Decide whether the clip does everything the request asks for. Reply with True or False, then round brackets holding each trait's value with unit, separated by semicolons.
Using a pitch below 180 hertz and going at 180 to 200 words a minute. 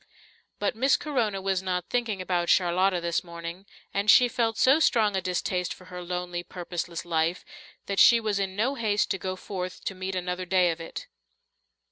False (185 Hz; 185 wpm)